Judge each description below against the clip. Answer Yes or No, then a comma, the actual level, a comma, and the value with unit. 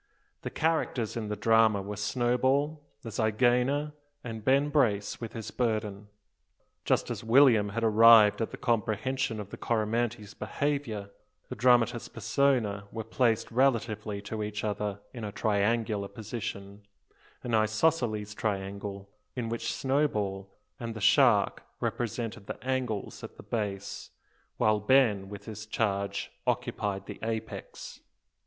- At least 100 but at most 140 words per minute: Yes, slow, 135 wpm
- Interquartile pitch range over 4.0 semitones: No, average, 2.8 semitones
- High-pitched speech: No, low, 110 Hz